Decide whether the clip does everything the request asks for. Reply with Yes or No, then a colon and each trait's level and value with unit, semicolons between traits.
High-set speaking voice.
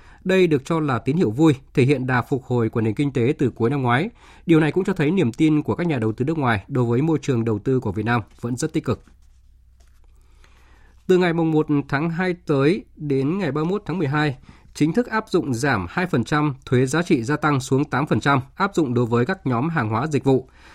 No: medium, 140 Hz